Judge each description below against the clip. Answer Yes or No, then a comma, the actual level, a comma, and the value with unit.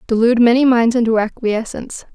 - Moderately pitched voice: No, high, 235 Hz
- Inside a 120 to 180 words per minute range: Yes, average, 140 wpm